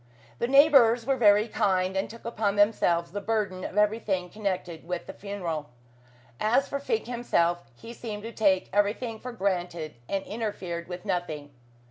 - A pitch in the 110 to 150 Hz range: No, high, 205 Hz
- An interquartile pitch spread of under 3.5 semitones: No, average, 4.1 semitones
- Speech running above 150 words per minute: Yes, average, 160 wpm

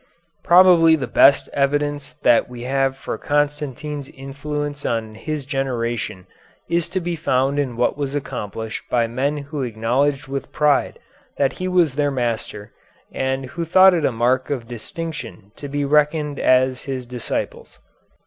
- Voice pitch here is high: No, medium, 140 Hz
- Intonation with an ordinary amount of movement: Yes, average, 3.0 semitones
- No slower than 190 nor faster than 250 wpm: No, average, 150 wpm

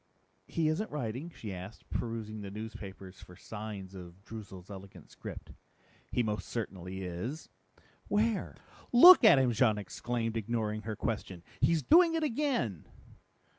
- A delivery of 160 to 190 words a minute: No, slow, 135 wpm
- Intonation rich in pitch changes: Yes, wide, 6.3 semitones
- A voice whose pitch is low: Yes, low, 110 Hz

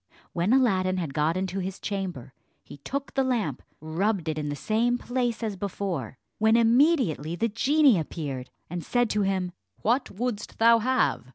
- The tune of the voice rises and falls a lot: Yes, wide, 6.2 semitones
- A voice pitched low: No, high, 200 Hz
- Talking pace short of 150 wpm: No, average, 170 wpm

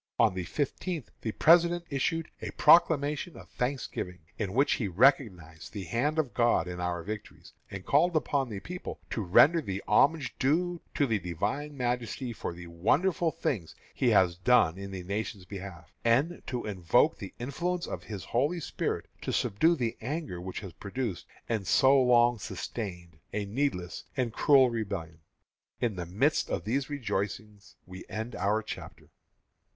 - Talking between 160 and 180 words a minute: Yes, average, 165 wpm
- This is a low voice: Yes, low, 115 Hz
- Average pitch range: No, wide, 6.7 semitones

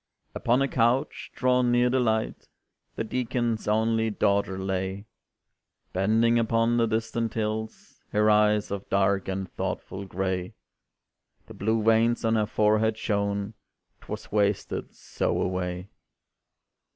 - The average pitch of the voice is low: Yes, low, 110 Hz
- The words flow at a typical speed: No, slow, 125 wpm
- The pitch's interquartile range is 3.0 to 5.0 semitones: No, narrow, 2.4 semitones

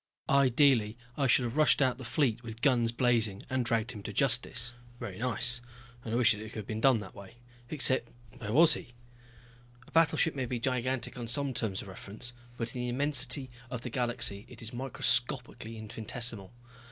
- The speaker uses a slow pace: No, average, 185 wpm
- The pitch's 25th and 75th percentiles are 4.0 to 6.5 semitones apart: No, average, 2.7 semitones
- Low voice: Yes, low, 120 Hz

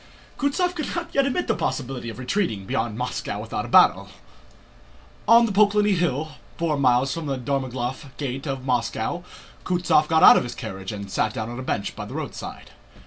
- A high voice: No, low, 135 Hz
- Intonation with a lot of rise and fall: Yes, wide, 7.0 semitones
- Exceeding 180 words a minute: Yes, average, 190 wpm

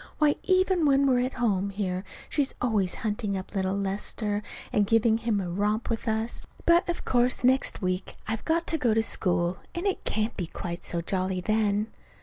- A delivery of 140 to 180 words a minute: No, average, 200 wpm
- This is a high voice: Yes, high, 215 Hz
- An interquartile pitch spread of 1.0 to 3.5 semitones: No, average, 4.5 semitones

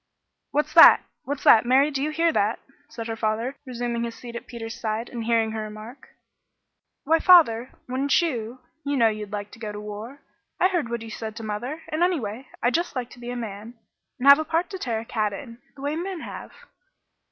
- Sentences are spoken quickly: Yes, fast, 220 wpm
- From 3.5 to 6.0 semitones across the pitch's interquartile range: Yes, average, 4.3 semitones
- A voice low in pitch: No, high, 240 Hz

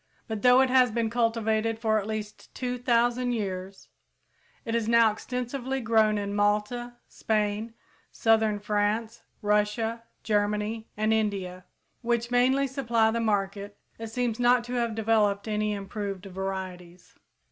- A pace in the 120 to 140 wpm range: Yes, slow, 135 wpm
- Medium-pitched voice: No, high, 220 Hz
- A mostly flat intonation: Yes, narrow, 2.3 semitones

